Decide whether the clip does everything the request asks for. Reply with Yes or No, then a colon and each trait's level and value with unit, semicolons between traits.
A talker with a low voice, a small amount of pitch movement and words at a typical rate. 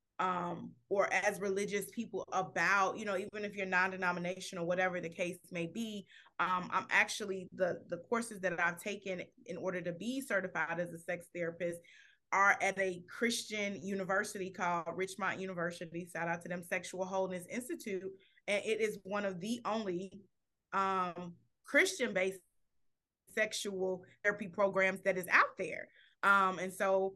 No: high, 190 Hz; narrow, 2.1 semitones; average, 160 wpm